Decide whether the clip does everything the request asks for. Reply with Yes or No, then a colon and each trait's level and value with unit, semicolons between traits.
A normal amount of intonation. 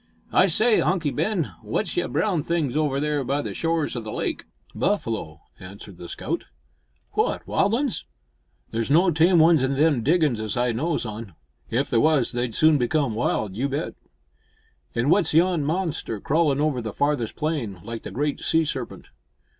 No: wide, 5.7 semitones